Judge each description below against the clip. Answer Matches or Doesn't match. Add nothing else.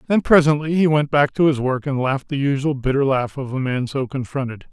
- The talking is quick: Matches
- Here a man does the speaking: Matches